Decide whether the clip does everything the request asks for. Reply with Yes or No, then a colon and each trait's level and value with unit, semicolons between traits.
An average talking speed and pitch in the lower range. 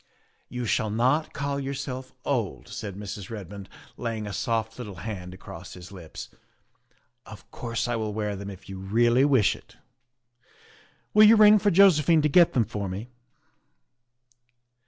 Yes: average, 165 wpm; low, 115 Hz